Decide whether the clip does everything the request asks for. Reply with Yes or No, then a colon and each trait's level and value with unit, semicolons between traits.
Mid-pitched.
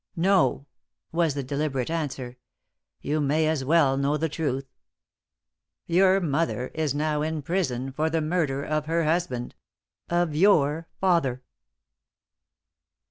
Yes: medium, 155 Hz